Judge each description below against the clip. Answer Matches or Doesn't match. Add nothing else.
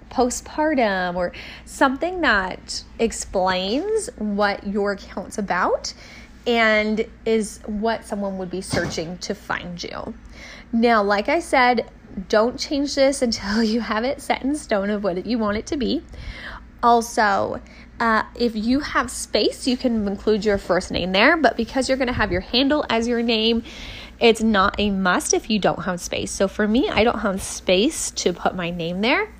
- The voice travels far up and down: Doesn't match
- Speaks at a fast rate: Doesn't match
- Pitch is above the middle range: Matches